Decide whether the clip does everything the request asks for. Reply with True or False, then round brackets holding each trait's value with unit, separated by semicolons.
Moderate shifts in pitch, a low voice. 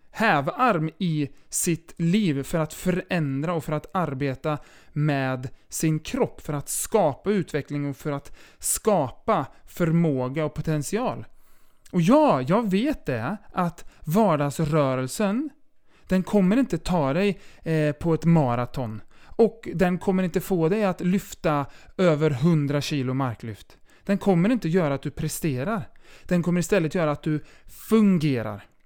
False (4.6 semitones; 160 Hz)